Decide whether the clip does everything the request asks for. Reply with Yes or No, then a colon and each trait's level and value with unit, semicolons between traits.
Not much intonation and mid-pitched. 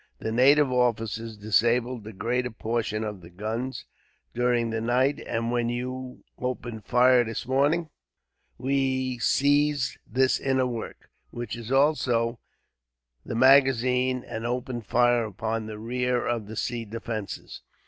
No: narrow, 2.2 semitones; low, 120 Hz